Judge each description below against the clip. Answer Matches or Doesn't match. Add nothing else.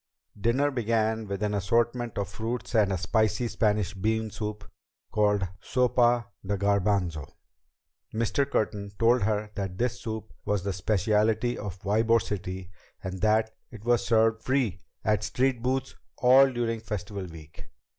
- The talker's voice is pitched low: Matches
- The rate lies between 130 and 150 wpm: Matches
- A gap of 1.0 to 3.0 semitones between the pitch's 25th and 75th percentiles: Matches